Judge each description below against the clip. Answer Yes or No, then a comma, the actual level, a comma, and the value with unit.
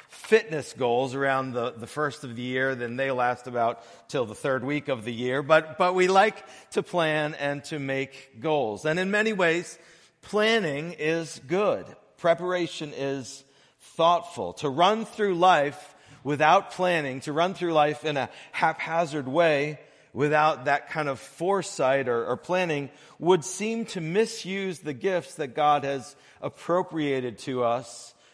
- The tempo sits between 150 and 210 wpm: Yes, average, 155 wpm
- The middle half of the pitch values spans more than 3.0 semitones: Yes, average, 4.5 semitones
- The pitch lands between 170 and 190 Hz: No, medium, 150 Hz